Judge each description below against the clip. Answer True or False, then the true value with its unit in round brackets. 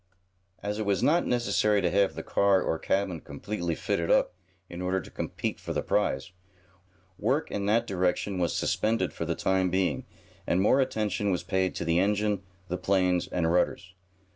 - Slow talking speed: False (180 wpm)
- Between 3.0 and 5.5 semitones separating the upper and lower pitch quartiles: False (2.6 semitones)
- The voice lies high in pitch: False (95 Hz)